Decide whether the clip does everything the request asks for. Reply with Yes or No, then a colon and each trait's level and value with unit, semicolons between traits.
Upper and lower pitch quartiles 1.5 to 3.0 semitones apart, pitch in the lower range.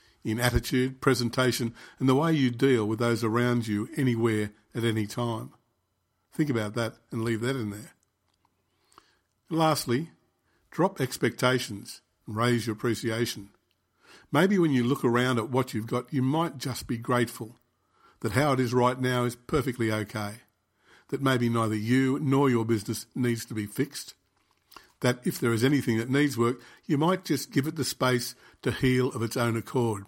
Yes: average, 2.7 semitones; low, 120 Hz